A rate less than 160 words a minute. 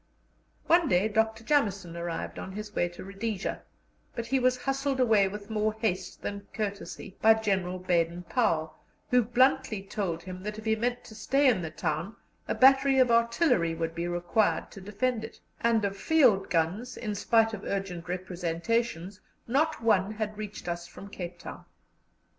No: average, 170 wpm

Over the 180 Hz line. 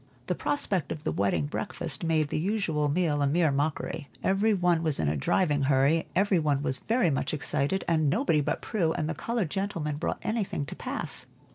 No: medium, 160 Hz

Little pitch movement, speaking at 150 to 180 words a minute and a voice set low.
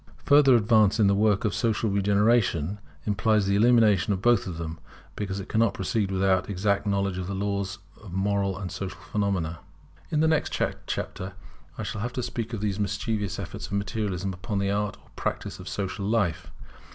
No: narrow, 2.1 semitones; average, 190 wpm; low, 100 Hz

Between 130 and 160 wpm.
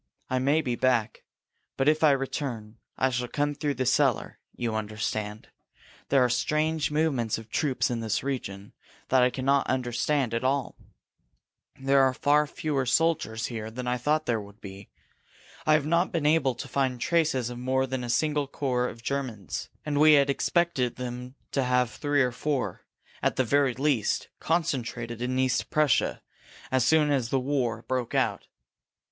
No: average, 175 wpm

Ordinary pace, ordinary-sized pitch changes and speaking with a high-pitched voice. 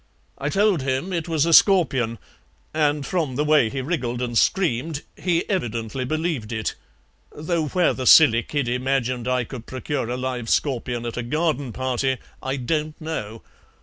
No: average, 165 wpm; average, 4.4 semitones; low, 135 Hz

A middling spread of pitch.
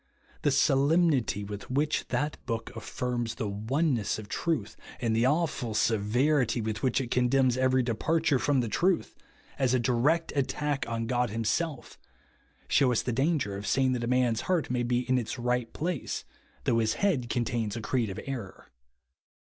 Yes: average, 3.4 semitones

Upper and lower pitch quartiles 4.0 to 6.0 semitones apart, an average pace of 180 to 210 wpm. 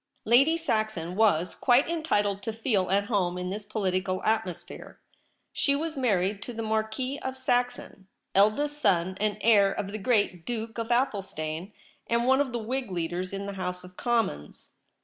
No: average, 4.5 semitones; average, 170 wpm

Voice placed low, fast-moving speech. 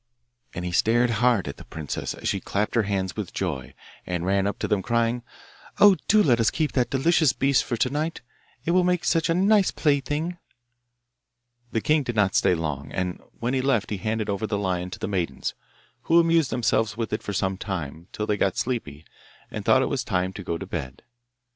Yes: low, 110 Hz; fast, 215 wpm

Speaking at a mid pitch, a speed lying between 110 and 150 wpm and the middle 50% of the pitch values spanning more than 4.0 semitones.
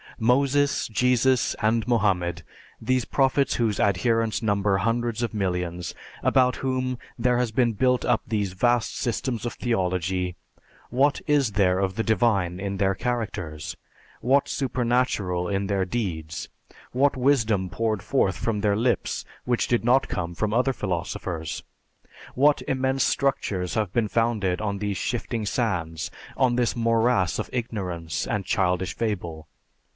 No: low, 110 Hz; average, 140 wpm; average, 4.7 semitones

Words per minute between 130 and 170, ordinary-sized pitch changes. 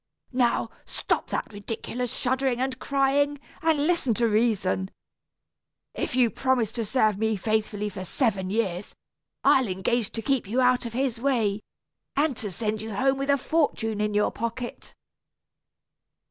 Yes: average, 150 wpm; average, 3.7 semitones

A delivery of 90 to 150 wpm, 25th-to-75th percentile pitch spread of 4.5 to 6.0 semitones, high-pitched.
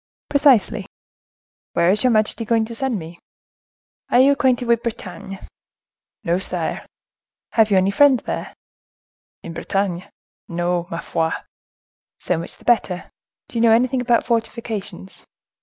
Yes: average, 140 wpm; average, 4.9 semitones; high, 215 Hz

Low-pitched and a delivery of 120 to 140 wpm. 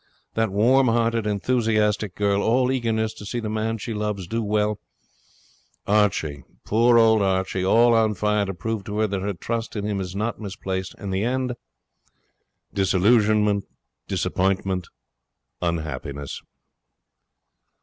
Yes: low, 105 Hz; slow, 135 wpm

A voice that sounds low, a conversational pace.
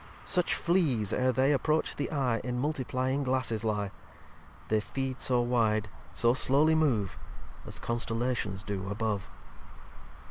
No: low, 125 Hz; slow, 130 wpm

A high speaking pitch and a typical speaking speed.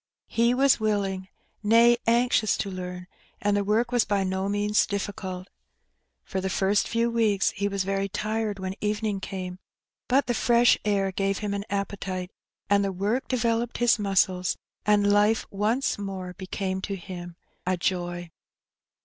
Yes: high, 200 Hz; average, 160 wpm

